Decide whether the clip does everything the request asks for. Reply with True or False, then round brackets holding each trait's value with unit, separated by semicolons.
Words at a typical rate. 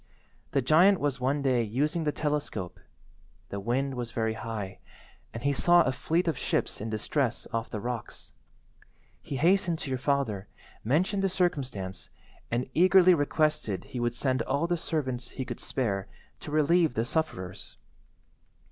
True (155 wpm)